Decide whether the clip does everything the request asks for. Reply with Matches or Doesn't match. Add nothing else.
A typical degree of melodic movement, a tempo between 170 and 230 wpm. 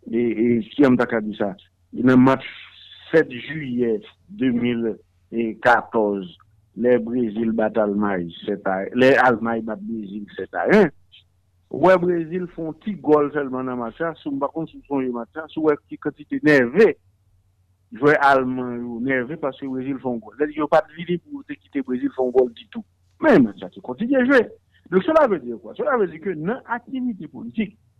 Doesn't match